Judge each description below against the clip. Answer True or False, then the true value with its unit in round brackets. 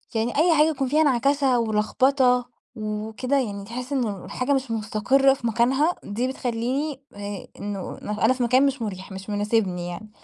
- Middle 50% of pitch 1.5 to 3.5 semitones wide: False (4.3 semitones)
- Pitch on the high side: True (240 Hz)